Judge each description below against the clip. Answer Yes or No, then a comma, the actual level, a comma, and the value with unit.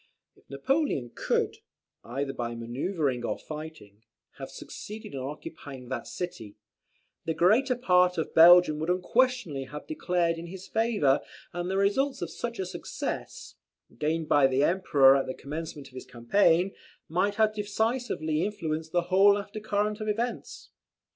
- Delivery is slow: No, average, 150 wpm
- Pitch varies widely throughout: Yes, wide, 6.5 semitones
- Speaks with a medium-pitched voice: Yes, medium, 175 Hz